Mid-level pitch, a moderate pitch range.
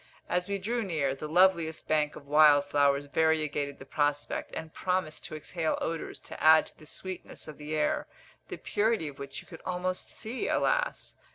Yes: medium, 155 Hz; average, 3.9 semitones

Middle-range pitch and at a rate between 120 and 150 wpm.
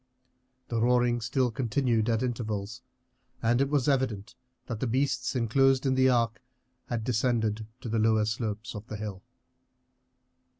No: low, 115 Hz; average, 145 wpm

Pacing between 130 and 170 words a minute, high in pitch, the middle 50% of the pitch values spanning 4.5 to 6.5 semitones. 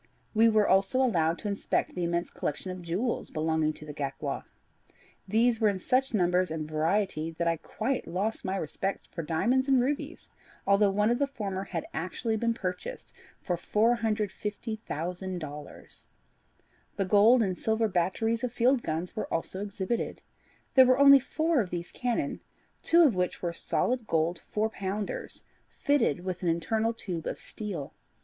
Yes: average, 160 wpm; high, 200 Hz; average, 5.1 semitones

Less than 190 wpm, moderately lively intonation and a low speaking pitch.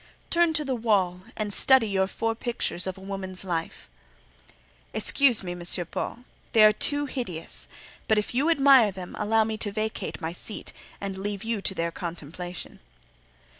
No: average, 170 wpm; average, 4.0 semitones; high, 210 Hz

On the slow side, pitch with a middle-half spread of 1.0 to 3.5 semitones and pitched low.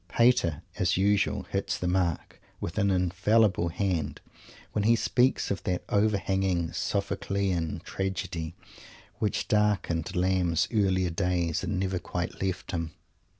Yes: slow, 125 wpm; narrow, 2.6 semitones; very low, 95 Hz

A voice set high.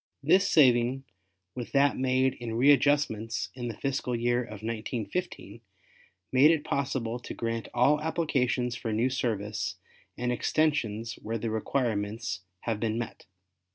No: low, 120 Hz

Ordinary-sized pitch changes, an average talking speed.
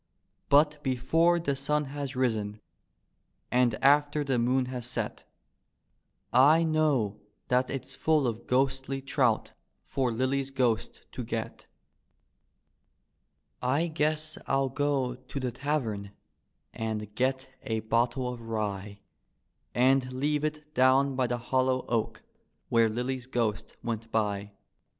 No: average, 3.1 semitones; slow, 120 wpm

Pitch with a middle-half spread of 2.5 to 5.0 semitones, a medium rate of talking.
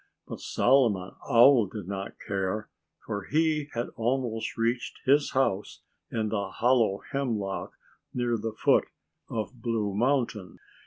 No: average, 3.8 semitones; slow, 125 wpm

